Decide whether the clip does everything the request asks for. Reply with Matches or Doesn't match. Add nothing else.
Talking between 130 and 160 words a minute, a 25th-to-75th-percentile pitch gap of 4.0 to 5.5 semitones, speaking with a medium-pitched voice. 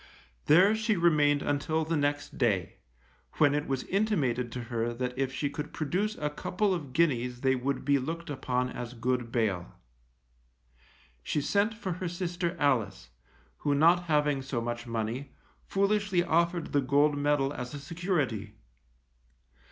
Matches